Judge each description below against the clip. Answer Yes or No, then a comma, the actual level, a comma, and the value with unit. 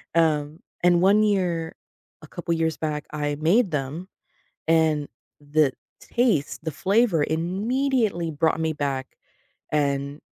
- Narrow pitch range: No, average, 3.7 semitones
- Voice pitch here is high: No, medium, 160 Hz